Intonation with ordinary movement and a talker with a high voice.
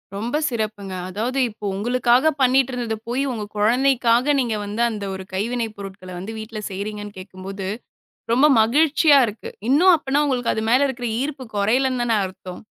Yes: average, 4.2 semitones; high, 235 Hz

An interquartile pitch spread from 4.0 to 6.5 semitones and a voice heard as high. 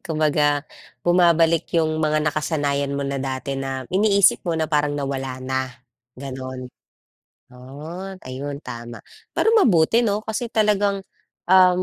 No: average, 5.2 semitones; medium, 155 Hz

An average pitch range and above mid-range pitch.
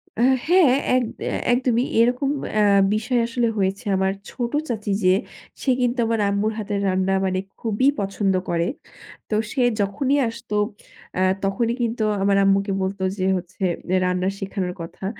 Yes: average, 3.7 semitones; high, 205 Hz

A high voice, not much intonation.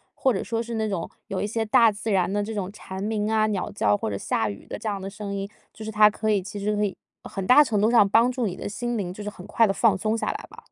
Yes: high, 210 Hz; narrow, 2.2 semitones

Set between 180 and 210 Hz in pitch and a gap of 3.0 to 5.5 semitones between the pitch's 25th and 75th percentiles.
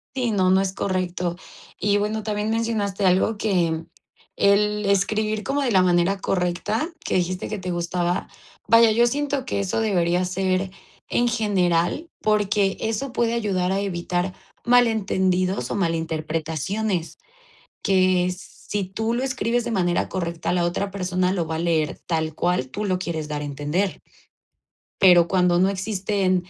Yes: high, 190 Hz; average, 3.3 semitones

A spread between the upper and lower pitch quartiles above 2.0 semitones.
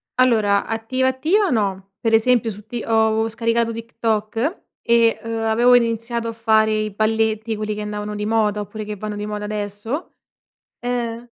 No: narrow, 1.7 semitones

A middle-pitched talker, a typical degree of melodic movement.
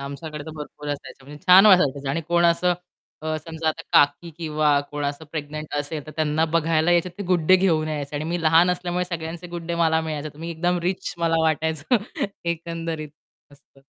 No: medium, 160 Hz; narrow, 2.2 semitones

